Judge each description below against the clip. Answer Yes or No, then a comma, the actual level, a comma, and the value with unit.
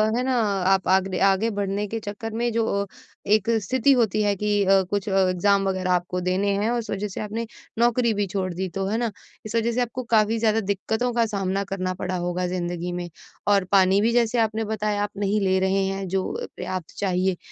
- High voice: Yes, high, 200 Hz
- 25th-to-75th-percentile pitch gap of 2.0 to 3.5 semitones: Yes, average, 2.9 semitones